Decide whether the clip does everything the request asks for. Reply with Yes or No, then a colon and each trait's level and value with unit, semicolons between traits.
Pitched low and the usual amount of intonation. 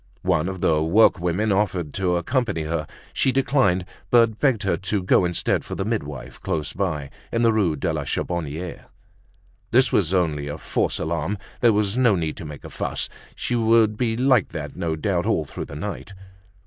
No: very low, 95 Hz; wide, 5.7 semitones